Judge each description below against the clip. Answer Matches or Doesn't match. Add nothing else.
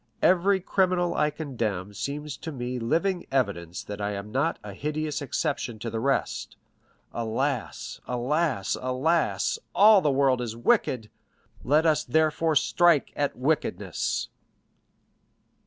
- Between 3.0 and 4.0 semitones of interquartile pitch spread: Doesn't match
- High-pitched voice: Doesn't match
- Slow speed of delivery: Matches